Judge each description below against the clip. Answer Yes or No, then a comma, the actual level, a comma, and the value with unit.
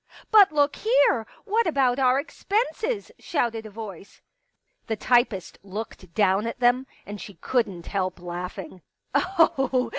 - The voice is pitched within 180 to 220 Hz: No, high, 230 Hz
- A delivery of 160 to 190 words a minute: No, average, 140 wpm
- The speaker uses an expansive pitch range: Yes, wide, 6.5 semitones